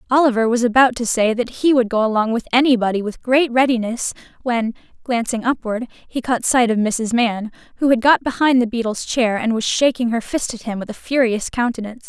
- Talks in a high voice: Yes, high, 235 Hz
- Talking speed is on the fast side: Yes, fast, 210 wpm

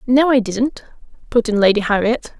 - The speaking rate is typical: Yes, average, 175 wpm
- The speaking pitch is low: No, high, 235 Hz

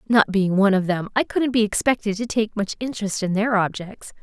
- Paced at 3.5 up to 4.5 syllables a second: No, 5.6 syllables/s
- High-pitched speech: Yes, high, 210 Hz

